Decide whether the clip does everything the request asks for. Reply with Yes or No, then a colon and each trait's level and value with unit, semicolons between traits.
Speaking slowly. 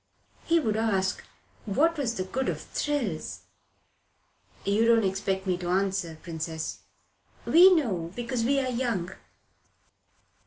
Yes: slow, 120 wpm